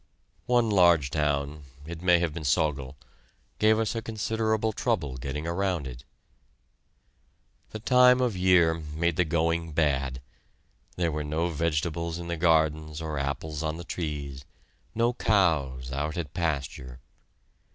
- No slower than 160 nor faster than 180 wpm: No, slow, 135 wpm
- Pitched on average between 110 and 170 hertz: No, very low, 80 Hz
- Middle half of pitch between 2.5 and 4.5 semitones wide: Yes, average, 3.3 semitones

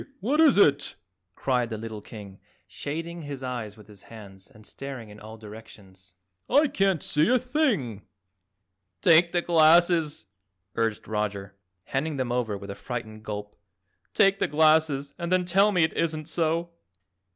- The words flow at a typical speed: Yes, average, 155 wpm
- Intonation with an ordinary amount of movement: No, wide, 7.8 semitones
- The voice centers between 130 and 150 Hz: Yes, medium, 140 Hz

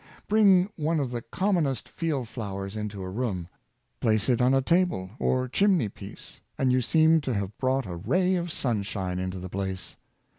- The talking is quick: No, average, 180 wpm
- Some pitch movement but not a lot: No, wide, 8.4 semitones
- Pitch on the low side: Yes, low, 125 Hz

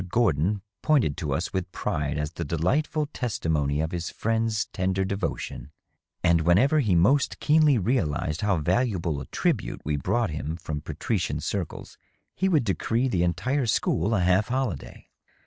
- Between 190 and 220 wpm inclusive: No, average, 155 wpm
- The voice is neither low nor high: No, very low, 95 Hz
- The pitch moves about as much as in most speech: No, wide, 6.5 semitones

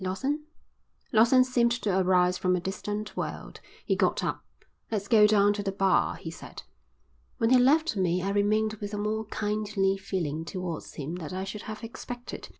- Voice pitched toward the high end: Yes, high, 205 Hz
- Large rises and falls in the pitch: No, average, 2.8 semitones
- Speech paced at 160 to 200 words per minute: Yes, average, 180 wpm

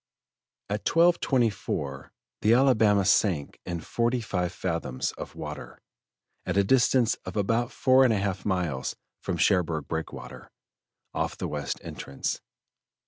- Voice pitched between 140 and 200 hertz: No, low, 100 Hz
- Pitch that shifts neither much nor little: No, wide, 6.1 semitones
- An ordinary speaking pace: No, slow, 130 wpm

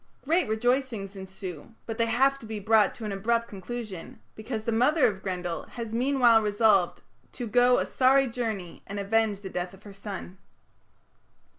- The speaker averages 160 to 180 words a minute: Yes, average, 170 wpm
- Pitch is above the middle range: Yes, high, 220 Hz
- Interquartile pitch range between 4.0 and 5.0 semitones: No, average, 3.6 semitones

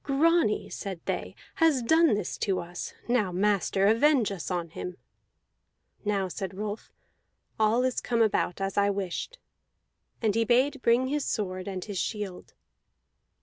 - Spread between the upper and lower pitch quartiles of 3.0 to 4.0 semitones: No, average, 4.5 semitones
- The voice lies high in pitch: Yes, high, 210 Hz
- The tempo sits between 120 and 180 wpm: Yes, average, 145 wpm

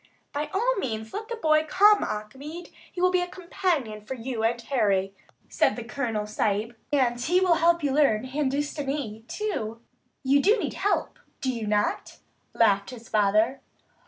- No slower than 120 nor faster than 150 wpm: No, average, 160 wpm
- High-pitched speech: Yes, very high, 265 Hz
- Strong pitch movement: Yes, wide, 7.1 semitones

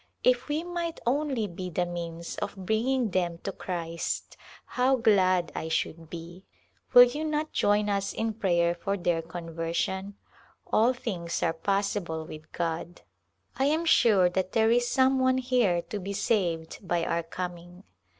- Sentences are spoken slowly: No, average, 160 wpm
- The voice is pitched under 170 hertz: No, high, 190 Hz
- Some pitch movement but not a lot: No, wide, 6.0 semitones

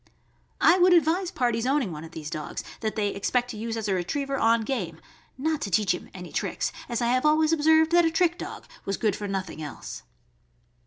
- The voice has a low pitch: No, high, 235 Hz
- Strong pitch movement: Yes, wide, 8.0 semitones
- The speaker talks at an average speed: No, fast, 215 wpm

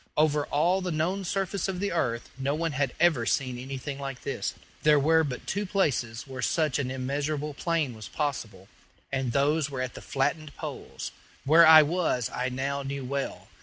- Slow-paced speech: No, average, 185 wpm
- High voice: No, medium, 140 Hz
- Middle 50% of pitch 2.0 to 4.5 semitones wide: Yes, average, 3.5 semitones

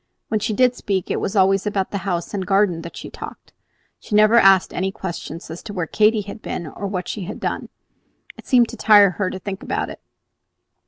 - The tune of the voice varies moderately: No, narrow, 2.3 semitones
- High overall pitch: Yes, high, 195 Hz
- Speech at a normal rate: No, fast, 225 wpm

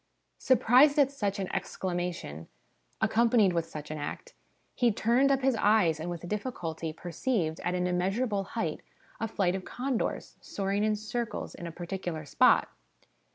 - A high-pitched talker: Yes, high, 195 Hz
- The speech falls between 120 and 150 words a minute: No, average, 160 wpm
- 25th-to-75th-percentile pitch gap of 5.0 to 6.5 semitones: Yes, wide, 5.4 semitones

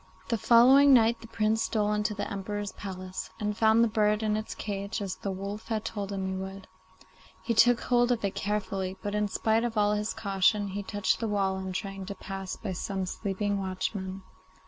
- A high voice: Yes, high, 205 Hz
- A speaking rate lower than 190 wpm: No, fast, 205 wpm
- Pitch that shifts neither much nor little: No, narrow, 2.2 semitones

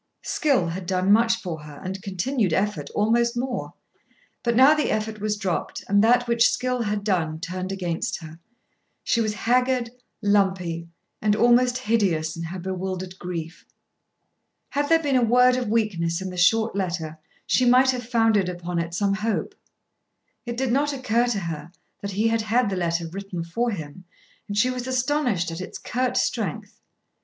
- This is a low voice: No, high, 205 Hz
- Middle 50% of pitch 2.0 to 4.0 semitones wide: No, average, 5.2 semitones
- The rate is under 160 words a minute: No, average, 175 wpm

